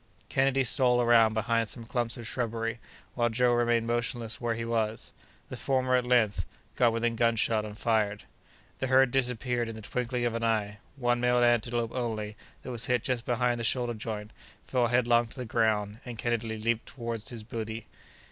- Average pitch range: No, narrow, 1.6 semitones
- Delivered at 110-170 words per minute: No, average, 185 wpm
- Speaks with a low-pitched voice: Yes, low, 115 Hz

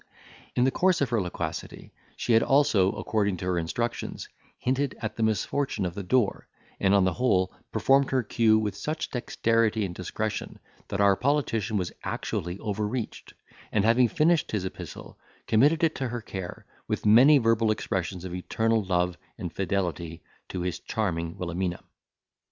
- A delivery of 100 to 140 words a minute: No, average, 165 wpm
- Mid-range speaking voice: No, low, 105 Hz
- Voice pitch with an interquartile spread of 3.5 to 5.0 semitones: Yes, average, 4.7 semitones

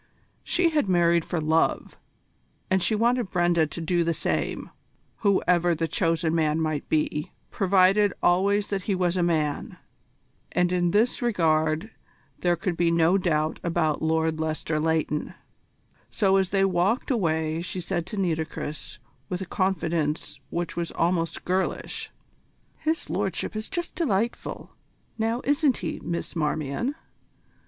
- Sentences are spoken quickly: No, average, 140 wpm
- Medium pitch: Yes, medium, 175 Hz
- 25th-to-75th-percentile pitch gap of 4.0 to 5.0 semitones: No, average, 3.4 semitones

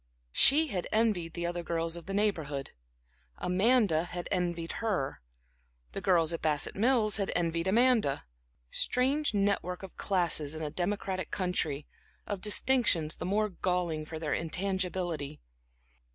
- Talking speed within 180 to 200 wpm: No, average, 140 wpm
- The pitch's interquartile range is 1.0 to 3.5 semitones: No, average, 3.9 semitones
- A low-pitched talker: No, medium, 180 Hz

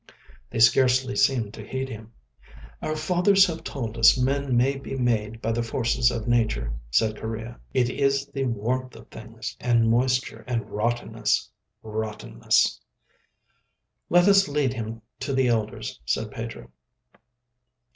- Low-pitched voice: Yes, low, 120 Hz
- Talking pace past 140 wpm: No, slow, 135 wpm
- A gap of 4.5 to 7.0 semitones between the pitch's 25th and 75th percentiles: No, average, 3.1 semitones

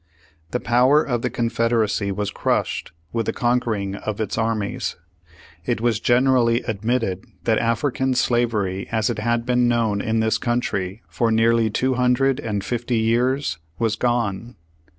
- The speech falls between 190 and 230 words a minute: No, average, 150 wpm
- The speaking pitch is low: Yes, low, 115 Hz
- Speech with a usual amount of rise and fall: No, narrow, 2.1 semitones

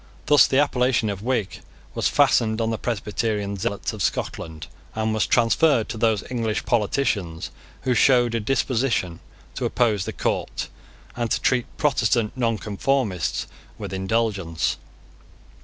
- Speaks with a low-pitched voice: Yes, low, 110 Hz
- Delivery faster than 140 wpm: No, slow, 135 wpm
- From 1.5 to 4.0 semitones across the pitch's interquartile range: Yes, average, 3.4 semitones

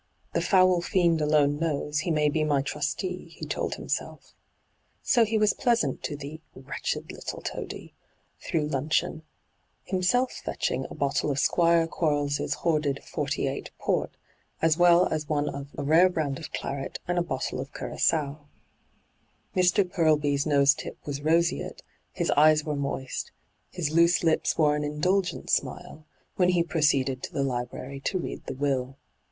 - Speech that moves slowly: No, average, 160 wpm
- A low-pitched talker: No, medium, 155 Hz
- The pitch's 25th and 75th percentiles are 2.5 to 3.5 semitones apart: Yes, average, 3.2 semitones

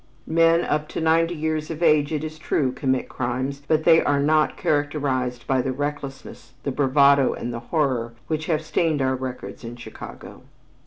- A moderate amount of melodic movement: Yes, average, 3.1 semitones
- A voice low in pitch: No, medium, 145 Hz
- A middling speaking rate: Yes, average, 175 wpm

